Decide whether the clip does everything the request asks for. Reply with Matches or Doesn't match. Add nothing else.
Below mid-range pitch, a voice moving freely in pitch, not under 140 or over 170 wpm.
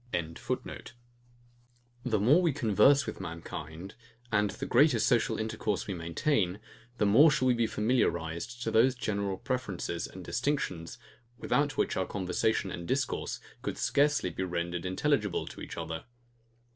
Matches